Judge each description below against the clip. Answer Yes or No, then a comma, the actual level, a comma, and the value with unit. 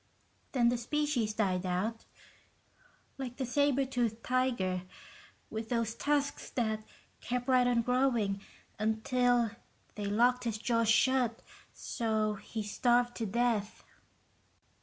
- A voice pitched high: Yes, high, 235 Hz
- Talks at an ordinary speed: No, slow, 115 wpm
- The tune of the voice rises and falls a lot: No, narrow, 2.4 semitones